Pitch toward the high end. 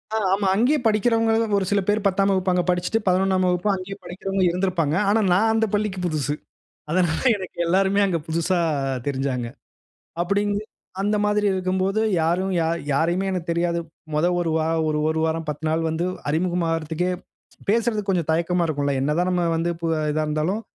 No: medium, 180 Hz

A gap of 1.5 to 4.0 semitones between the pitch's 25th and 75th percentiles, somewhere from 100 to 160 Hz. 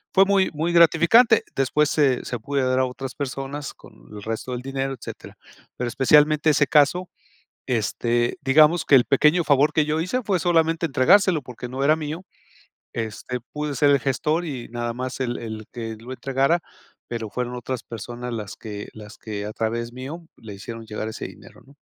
No: average, 4.4 semitones; low, 135 Hz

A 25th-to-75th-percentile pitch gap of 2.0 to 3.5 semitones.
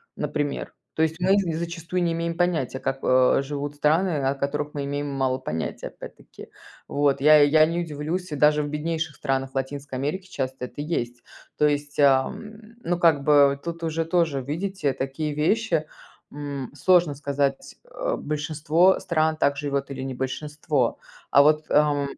Yes: average, 2.9 semitones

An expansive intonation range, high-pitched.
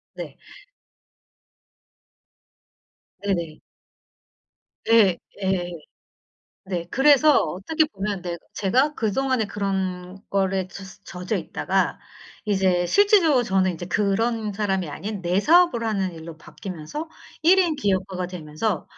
No: average, 4.5 semitones; high, 195 Hz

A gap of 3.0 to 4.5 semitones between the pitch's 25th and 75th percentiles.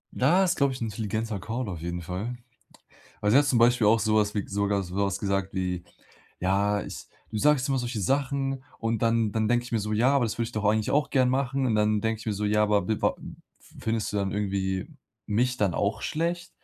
Yes: average, 3.6 semitones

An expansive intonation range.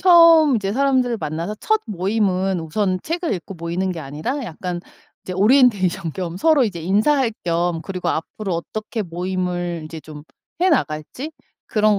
Yes: wide, 6.3 semitones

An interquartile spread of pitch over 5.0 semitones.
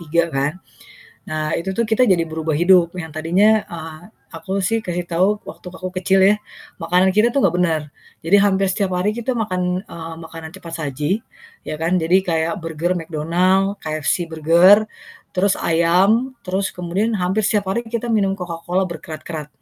No: average, 3.1 semitones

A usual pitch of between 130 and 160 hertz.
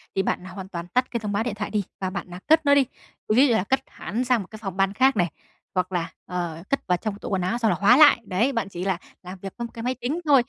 No: high, 205 Hz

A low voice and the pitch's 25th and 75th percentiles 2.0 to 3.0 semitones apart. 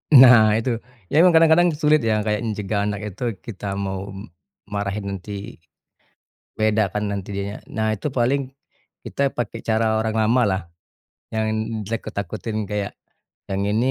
Yes: low, 110 Hz; average, 2.7 semitones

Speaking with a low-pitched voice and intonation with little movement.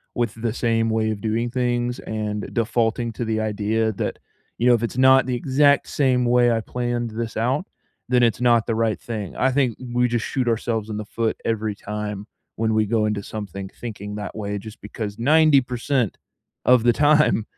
Yes: low, 115 Hz; narrow, 2.2 semitones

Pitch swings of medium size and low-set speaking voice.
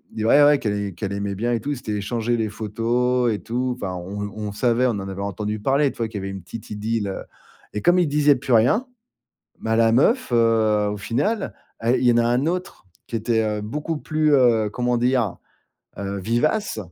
Yes: average, 3.6 semitones; low, 115 Hz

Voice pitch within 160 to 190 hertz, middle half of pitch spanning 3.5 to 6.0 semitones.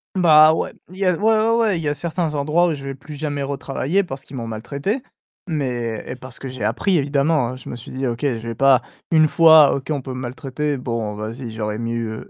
No: medium, 140 Hz; average, 4.6 semitones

